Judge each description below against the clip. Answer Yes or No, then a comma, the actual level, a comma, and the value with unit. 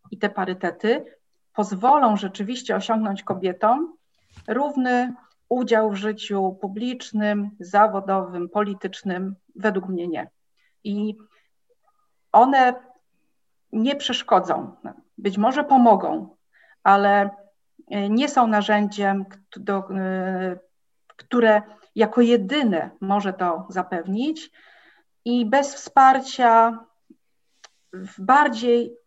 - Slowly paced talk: Yes, slow, 80 wpm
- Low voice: No, high, 215 Hz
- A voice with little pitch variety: No, average, 3.9 semitones